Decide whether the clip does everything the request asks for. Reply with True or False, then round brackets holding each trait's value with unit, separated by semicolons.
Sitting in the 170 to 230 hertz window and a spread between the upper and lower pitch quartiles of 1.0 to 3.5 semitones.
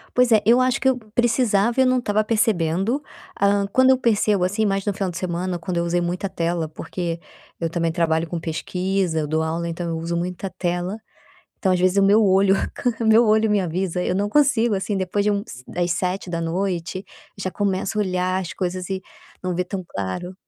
True (185 Hz; 3.2 semitones)